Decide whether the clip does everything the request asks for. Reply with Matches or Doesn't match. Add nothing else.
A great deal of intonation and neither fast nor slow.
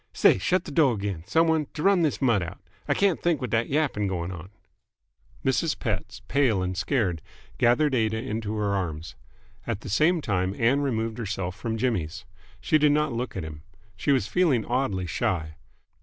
Matches